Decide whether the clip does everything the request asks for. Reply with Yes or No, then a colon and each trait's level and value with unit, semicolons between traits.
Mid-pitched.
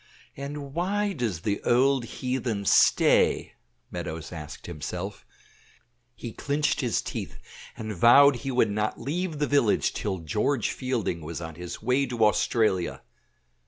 No: low, 120 Hz